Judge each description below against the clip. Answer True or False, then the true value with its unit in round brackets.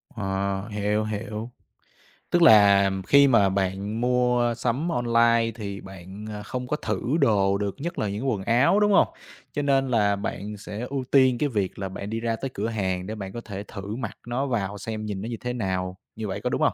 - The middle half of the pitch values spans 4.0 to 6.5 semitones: False (3.5 semitones)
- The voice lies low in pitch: True (110 Hz)